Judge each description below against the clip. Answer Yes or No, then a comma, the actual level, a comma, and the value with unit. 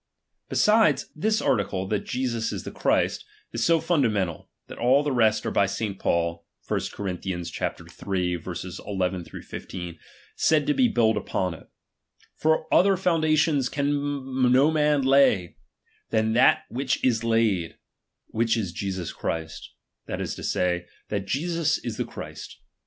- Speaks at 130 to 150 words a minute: Yes, average, 140 wpm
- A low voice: Yes, low, 115 Hz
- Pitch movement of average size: No, wide, 7.5 semitones